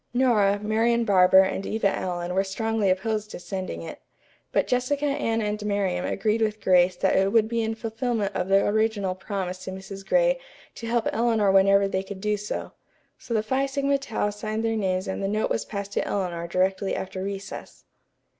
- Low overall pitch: No, high, 205 Hz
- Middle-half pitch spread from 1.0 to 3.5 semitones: Yes, average, 2.8 semitones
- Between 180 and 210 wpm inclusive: Yes, average, 190 wpm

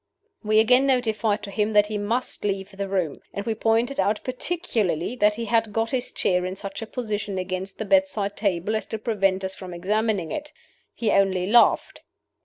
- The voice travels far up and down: No, average, 2.7 semitones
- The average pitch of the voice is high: Yes, high, 210 Hz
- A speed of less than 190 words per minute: No, average, 195 wpm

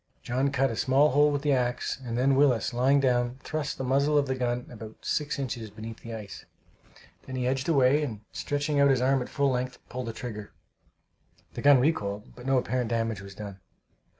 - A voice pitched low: Yes, low, 130 Hz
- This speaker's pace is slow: No, fast, 205 wpm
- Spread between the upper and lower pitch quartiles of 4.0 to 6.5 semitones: No, average, 3.1 semitones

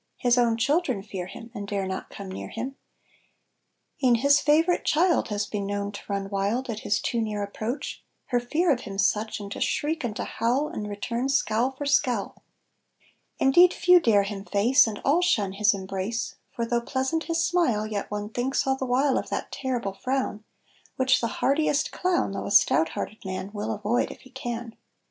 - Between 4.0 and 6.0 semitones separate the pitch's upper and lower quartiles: Yes, average, 4.6 semitones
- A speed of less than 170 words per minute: No, average, 195 wpm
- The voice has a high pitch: Yes, high, 235 Hz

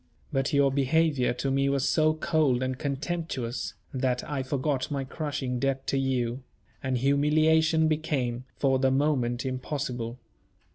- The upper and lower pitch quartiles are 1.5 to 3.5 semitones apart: Yes, average, 2.7 semitones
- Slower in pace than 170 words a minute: Yes, average, 140 wpm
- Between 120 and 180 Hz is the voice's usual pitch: Yes, low, 135 Hz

